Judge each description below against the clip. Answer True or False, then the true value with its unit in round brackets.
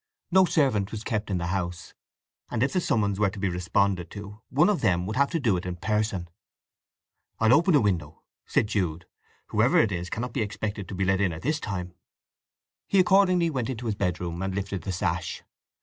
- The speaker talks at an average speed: False (210 wpm)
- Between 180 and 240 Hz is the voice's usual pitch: False (100 Hz)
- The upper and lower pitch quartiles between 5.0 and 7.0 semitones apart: True (5.3 semitones)